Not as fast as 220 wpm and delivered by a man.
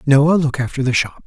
No: fast, 235 wpm; male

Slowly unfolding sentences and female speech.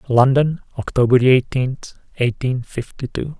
No: slow, 105 wpm; male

